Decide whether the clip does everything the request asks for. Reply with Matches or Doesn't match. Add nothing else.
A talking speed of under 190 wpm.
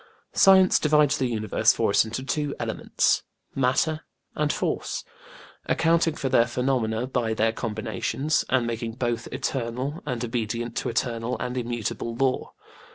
Matches